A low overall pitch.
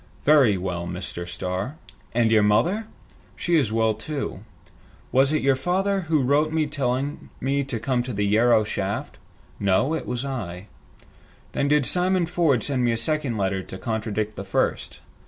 Yes: low, 125 Hz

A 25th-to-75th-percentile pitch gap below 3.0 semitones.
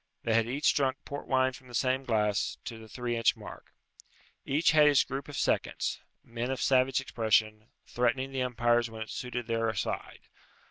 Yes: narrow, 2.6 semitones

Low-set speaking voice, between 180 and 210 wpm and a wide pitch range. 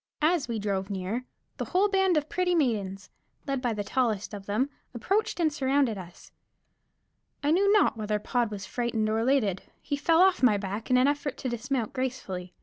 No: high, 245 Hz; average, 190 wpm; wide, 5.8 semitones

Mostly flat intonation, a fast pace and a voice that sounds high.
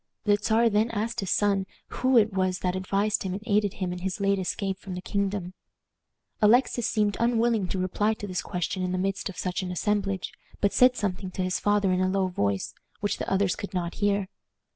Yes: narrow, 2.1 semitones; fast, 215 wpm; high, 195 Hz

